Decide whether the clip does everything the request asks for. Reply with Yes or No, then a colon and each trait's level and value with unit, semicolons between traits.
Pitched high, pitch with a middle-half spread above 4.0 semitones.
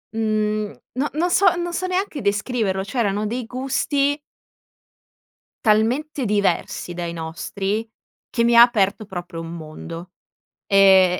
Yes: high, 215 Hz; average, 5.2 semitones